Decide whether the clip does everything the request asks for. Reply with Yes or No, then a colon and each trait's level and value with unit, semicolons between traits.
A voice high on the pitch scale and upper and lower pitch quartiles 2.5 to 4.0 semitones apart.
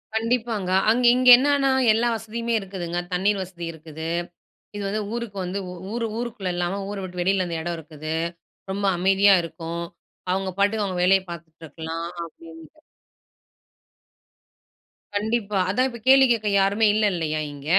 No: high, 195 Hz; average, 4.5 semitones